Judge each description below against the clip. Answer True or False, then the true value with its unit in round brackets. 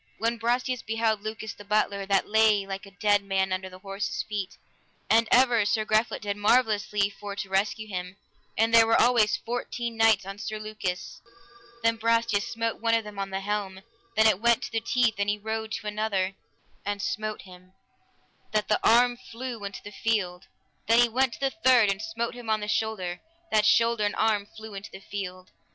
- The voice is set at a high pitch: True (215 Hz)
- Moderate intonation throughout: False (2.3 semitones)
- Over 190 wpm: True (200 wpm)